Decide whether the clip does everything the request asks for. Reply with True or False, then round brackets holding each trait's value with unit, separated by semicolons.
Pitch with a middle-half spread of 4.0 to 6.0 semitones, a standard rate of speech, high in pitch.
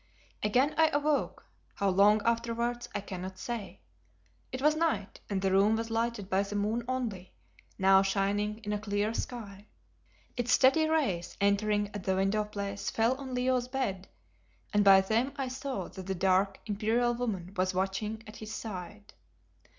False (3.6 semitones; 165 wpm; 210 Hz)